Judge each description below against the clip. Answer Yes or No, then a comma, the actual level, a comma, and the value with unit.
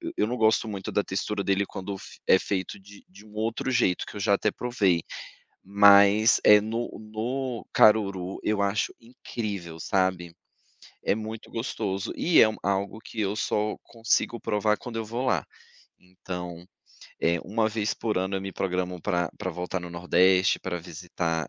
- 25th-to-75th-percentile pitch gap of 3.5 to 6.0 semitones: No, average, 2.9 semitones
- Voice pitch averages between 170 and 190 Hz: No, low, 100 Hz